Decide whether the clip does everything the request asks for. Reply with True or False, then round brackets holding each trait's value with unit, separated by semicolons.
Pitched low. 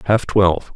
True (95 Hz)